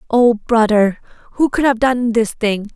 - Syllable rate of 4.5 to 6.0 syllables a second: No, 4.3 syllables/s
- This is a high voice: Yes, high, 230 Hz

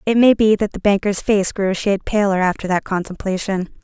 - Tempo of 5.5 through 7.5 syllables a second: Yes, 5.8 syllables/s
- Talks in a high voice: Yes, high, 200 Hz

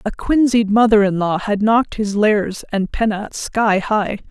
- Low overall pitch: No, high, 210 Hz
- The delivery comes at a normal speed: Yes, average, 180 wpm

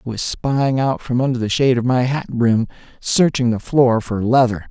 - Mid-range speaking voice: No, low, 125 Hz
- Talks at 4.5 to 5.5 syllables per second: Yes, 5.0 syllables/s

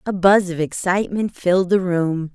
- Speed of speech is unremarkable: Yes, average, 180 wpm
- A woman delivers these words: Yes, female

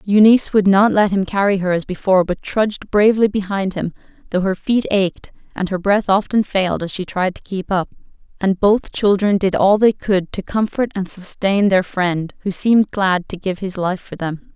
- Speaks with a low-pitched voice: No, high, 195 Hz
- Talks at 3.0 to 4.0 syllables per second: No, 5.0 syllables/s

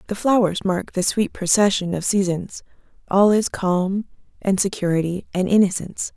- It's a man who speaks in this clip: No, female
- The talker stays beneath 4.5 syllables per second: No, 5.0 syllables/s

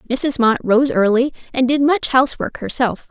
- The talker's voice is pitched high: Yes, very high, 255 Hz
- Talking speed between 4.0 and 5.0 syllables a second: Yes, 4.9 syllables/s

